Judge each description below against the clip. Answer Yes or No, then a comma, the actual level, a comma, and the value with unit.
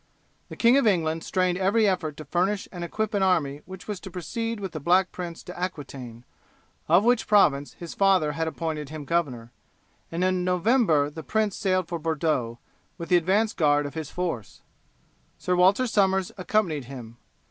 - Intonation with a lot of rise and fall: No, average, 4.0 semitones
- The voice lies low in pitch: No, medium, 175 Hz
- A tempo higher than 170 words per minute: Yes, average, 180 wpm